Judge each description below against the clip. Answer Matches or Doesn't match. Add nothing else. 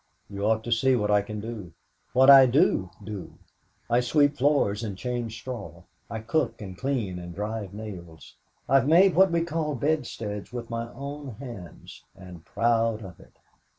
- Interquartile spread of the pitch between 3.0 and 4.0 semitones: Doesn't match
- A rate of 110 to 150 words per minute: Doesn't match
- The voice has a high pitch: Doesn't match